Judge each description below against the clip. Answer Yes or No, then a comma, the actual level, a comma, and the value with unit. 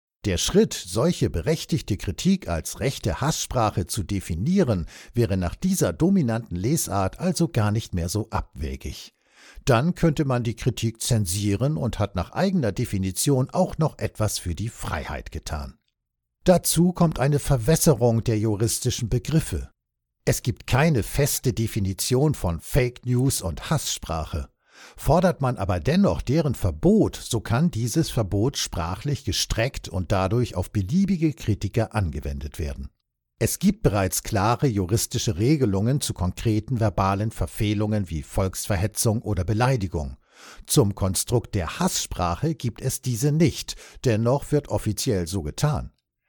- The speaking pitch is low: Yes, low, 110 Hz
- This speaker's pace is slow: Yes, slow, 130 wpm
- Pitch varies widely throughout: Yes, wide, 6.1 semitones